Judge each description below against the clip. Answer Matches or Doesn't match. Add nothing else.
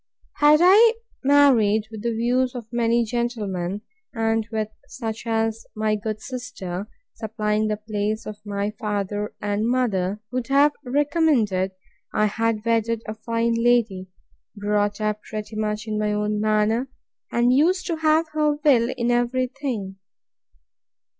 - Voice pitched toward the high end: Matches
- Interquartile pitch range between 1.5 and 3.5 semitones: Matches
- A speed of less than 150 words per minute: Matches